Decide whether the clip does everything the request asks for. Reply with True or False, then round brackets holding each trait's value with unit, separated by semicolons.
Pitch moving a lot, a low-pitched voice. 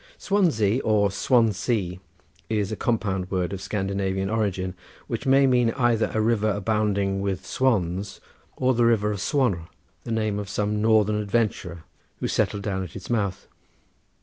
False (2.7 semitones; 105 Hz)